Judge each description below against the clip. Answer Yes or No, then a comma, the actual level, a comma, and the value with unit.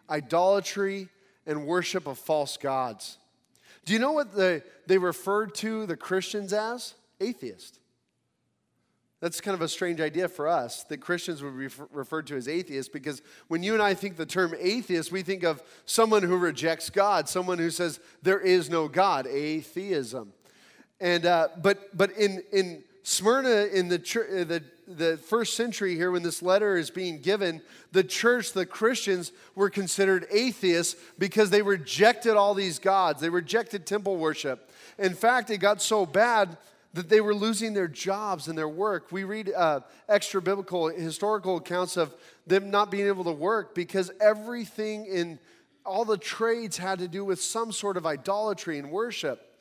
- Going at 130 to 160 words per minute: No, average, 170 wpm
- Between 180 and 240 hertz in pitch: Yes, high, 190 Hz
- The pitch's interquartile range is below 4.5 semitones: Yes, average, 3.5 semitones